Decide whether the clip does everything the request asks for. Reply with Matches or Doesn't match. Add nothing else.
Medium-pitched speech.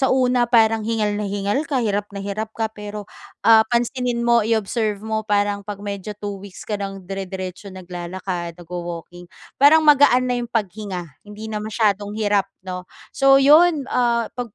Doesn't match